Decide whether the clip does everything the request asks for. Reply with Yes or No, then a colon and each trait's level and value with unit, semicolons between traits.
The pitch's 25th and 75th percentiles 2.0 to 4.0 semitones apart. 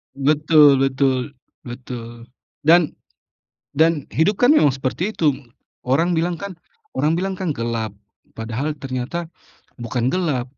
No: average, 4.8 semitones